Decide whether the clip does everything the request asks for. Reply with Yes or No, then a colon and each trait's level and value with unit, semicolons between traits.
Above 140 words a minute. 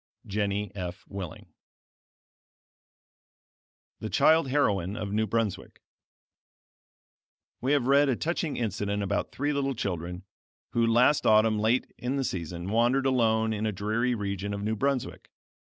No: slow, 135 wpm